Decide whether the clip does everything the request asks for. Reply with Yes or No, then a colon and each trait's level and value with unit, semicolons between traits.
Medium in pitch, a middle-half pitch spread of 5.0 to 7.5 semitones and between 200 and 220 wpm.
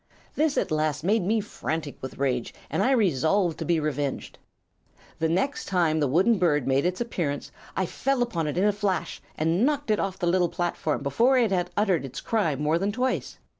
Yes: medium, 175 Hz; wide, 5.5 semitones; fast, 205 wpm